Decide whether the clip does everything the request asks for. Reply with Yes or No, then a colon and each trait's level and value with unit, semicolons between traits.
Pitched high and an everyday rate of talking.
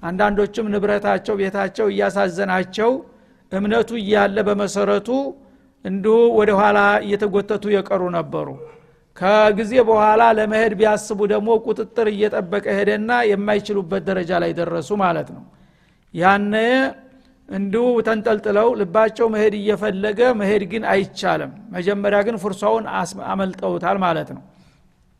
Yes: high, 210 Hz; average, 100 wpm